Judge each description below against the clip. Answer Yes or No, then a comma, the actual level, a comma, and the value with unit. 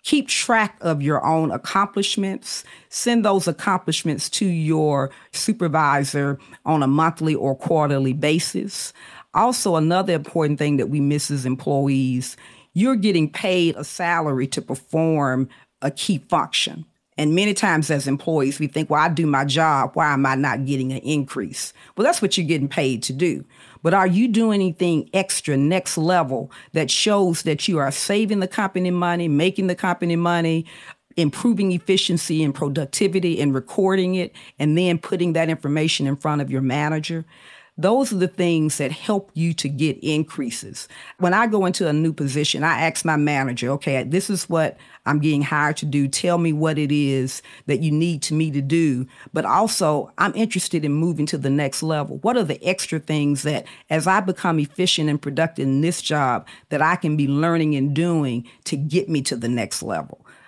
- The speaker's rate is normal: Yes, average, 180 wpm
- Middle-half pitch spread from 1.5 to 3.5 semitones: No, average, 3.9 semitones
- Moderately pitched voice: Yes, medium, 160 Hz